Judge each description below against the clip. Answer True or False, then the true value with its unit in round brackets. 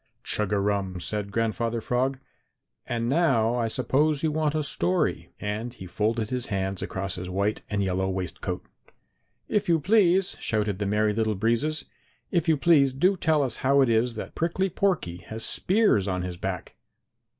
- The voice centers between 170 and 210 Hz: False (115 Hz)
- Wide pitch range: True (6.9 semitones)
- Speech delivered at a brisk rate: False (175 wpm)